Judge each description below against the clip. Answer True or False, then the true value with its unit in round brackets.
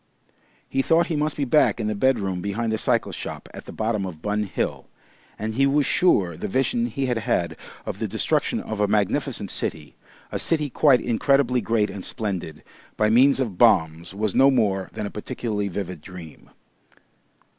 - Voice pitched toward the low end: True (110 Hz)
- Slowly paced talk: False (185 wpm)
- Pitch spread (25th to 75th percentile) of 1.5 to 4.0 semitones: False (5.4 semitones)